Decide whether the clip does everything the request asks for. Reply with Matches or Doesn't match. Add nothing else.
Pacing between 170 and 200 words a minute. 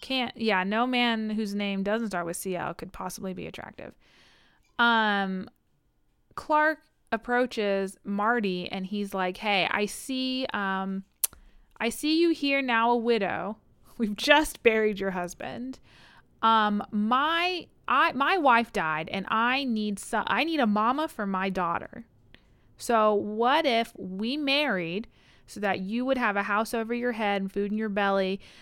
Doesn't match